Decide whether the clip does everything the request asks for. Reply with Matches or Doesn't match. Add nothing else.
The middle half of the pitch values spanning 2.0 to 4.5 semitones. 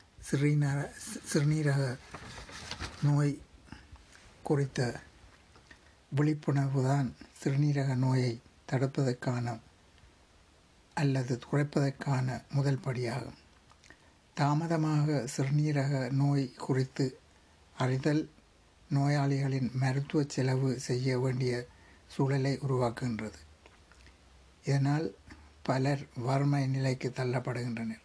Matches